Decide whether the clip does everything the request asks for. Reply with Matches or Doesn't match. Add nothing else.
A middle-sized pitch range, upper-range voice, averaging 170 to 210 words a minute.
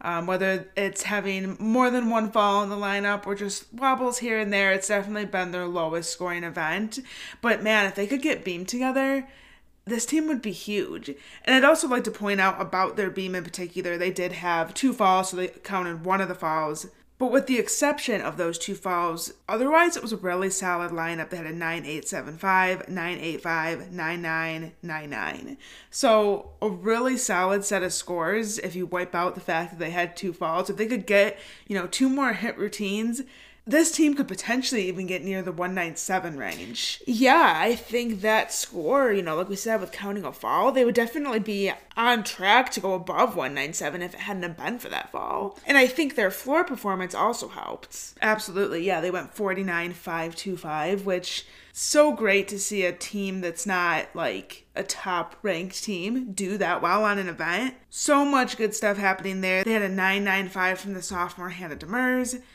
Matches